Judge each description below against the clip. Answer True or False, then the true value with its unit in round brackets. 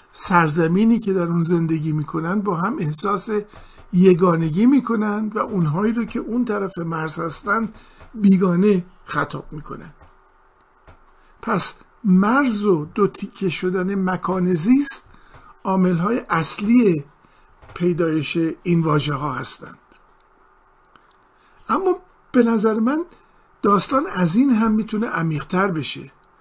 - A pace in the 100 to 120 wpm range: True (115 wpm)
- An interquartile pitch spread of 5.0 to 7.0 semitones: False (4.3 semitones)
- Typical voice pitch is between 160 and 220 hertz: True (190 Hz)